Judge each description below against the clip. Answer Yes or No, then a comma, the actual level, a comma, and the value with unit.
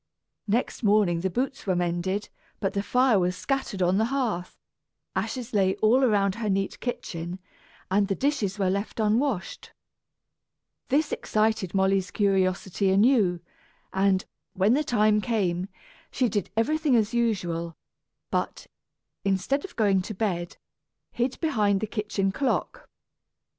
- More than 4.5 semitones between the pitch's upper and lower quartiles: No, average, 3.8 semitones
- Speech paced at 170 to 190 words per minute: No, slow, 135 wpm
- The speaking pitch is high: Yes, high, 205 Hz